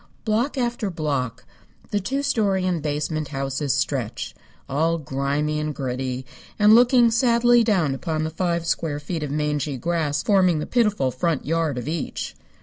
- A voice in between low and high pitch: Yes, medium, 160 Hz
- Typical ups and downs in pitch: No, wide, 6.3 semitones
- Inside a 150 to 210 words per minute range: Yes, average, 155 wpm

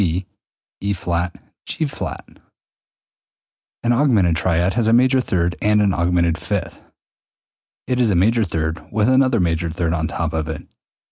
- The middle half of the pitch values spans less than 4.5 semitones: No, wide, 5.4 semitones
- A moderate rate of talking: Yes, average, 150 wpm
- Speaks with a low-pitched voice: Yes, very low, 90 Hz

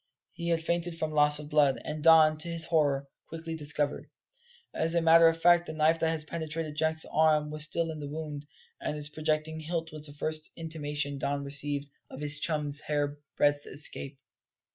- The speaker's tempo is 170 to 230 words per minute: Yes, average, 185 wpm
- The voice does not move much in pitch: Yes, narrow, 1.7 semitones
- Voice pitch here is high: No, medium, 155 Hz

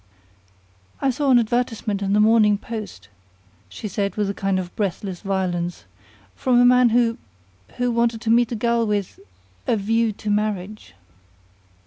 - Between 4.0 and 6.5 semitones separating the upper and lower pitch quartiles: No, average, 2.9 semitones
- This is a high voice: Yes, high, 215 Hz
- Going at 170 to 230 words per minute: No, average, 155 wpm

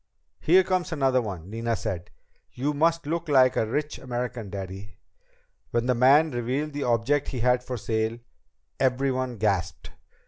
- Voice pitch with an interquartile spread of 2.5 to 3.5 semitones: No, average, 4.5 semitones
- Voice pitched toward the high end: No, low, 125 Hz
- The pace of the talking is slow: No, average, 150 wpm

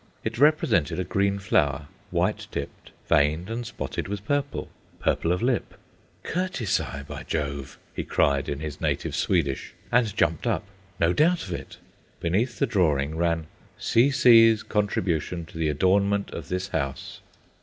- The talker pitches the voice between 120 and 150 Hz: No, very low, 90 Hz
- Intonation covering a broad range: Yes, wide, 6.7 semitones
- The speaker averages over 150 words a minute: No, average, 145 wpm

